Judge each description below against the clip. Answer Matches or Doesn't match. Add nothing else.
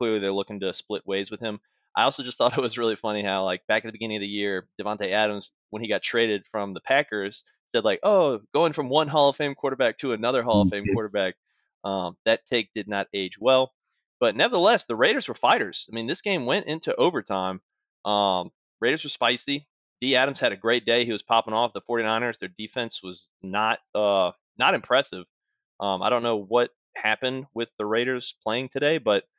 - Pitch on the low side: Matches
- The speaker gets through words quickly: Matches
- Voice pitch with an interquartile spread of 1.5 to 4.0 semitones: Matches